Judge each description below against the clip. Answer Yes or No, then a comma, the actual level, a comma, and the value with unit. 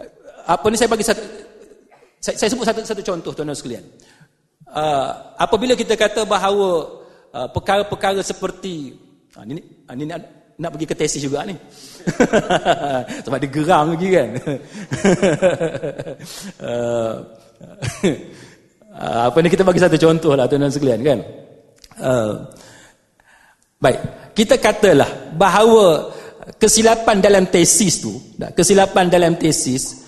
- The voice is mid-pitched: Yes, medium, 180 Hz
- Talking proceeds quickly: No, average, 120 wpm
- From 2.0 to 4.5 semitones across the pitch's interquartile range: No, wide, 5.7 semitones